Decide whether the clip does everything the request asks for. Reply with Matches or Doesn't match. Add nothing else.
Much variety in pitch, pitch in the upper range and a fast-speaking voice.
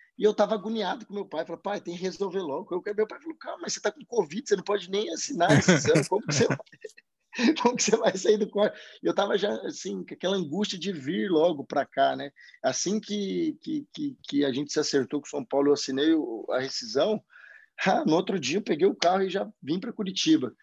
Matches